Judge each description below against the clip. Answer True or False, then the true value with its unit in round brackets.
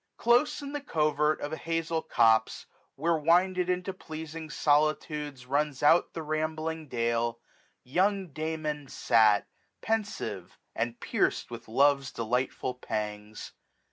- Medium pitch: True (150 Hz)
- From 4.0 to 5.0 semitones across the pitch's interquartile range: True (4.7 semitones)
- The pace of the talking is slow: True (125 wpm)